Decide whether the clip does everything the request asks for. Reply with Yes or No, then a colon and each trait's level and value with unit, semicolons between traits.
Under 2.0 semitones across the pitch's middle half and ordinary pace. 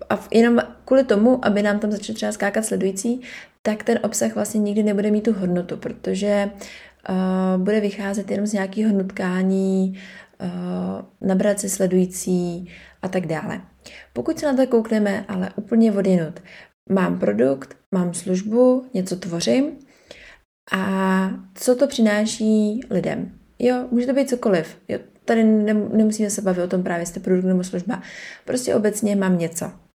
No: average, 2.8 semitones; average, 150 wpm